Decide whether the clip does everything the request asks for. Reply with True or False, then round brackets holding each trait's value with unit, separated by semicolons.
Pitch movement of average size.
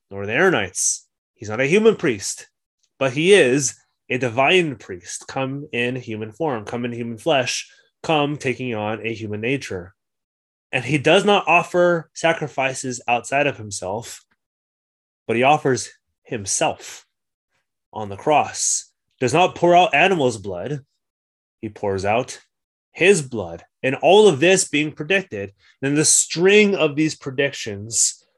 False (6.1 semitones)